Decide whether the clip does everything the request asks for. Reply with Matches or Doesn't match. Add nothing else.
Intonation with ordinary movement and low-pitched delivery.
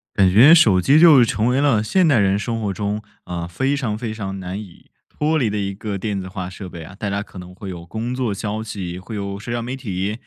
Matches